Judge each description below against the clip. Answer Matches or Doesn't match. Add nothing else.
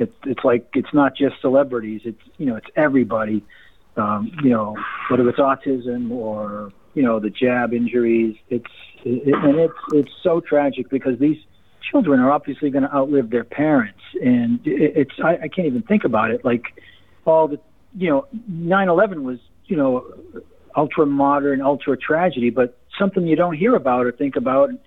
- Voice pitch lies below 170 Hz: Matches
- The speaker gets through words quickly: Doesn't match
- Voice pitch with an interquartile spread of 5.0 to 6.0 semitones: Matches